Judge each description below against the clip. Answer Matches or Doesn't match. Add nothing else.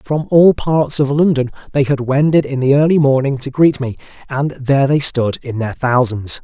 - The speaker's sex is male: Matches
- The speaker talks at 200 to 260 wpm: Matches